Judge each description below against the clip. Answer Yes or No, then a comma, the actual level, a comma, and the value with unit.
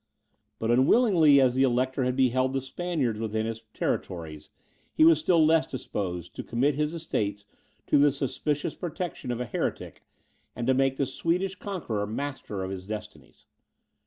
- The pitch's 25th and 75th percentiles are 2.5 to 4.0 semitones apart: No, wide, 5.5 semitones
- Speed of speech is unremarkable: Yes, average, 160 wpm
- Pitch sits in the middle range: No, low, 130 Hz